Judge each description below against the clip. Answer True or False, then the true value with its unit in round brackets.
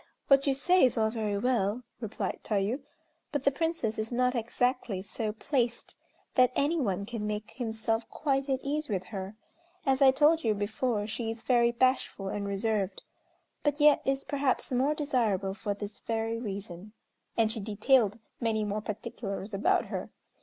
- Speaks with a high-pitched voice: True (225 Hz)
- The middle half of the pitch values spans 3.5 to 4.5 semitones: True (4.0 semitones)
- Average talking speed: True (165 wpm)